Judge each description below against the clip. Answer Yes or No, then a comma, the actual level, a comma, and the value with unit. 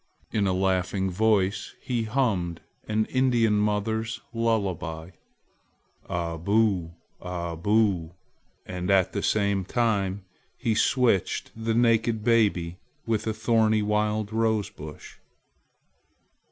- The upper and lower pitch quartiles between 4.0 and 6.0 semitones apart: No, average, 3.3 semitones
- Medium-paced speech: No, slow, 105 wpm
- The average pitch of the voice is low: Yes, low, 105 Hz